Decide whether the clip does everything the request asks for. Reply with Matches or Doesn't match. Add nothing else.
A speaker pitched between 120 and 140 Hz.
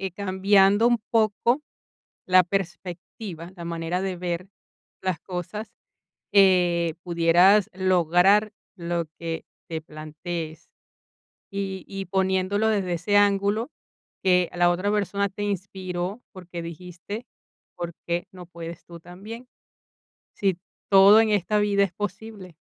Doesn't match